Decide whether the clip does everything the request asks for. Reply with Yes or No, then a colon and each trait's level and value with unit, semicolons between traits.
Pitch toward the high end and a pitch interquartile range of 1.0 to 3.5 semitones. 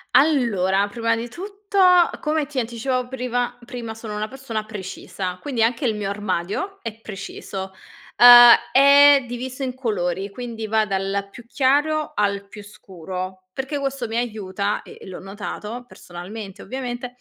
No: high, 230 Hz; average, 4.5 semitones